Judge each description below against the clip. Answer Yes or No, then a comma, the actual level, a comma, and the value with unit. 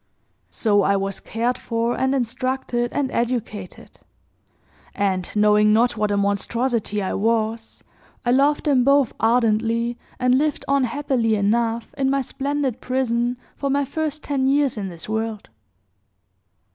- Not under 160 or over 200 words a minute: No, average, 140 wpm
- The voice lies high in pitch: Yes, high, 235 Hz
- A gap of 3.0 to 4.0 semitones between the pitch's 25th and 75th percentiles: Yes, average, 3.7 semitones